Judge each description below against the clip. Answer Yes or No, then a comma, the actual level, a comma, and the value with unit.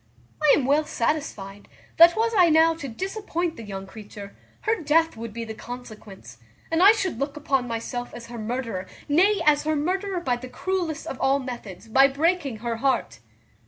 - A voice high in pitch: Yes, very high, 275 Hz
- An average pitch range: No, wide, 6.2 semitones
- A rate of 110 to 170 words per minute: No, average, 185 wpm